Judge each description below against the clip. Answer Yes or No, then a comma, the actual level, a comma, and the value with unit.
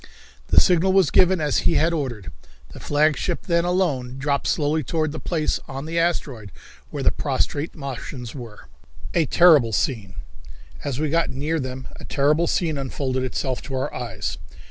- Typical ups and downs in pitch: Yes, average, 4.2 semitones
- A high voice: No, medium, 145 Hz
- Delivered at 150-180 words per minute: Yes, average, 165 wpm